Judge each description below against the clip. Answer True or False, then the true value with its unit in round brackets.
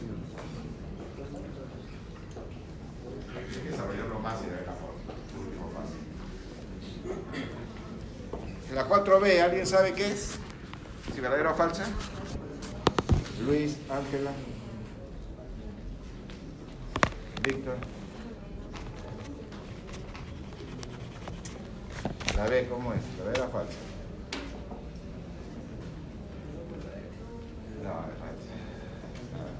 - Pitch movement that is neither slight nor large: False (6.1 semitones)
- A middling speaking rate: False (65 wpm)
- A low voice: True (125 Hz)